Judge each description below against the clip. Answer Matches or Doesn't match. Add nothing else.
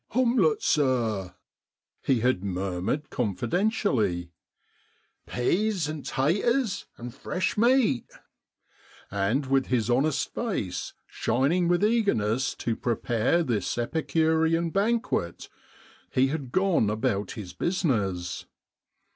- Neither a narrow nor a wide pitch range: Doesn't match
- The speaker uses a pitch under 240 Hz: Matches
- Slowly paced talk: Matches